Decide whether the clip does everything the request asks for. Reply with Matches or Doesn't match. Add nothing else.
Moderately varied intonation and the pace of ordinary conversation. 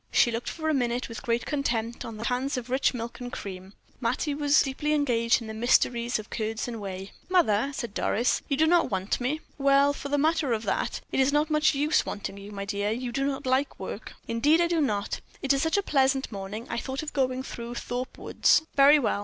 Doesn't match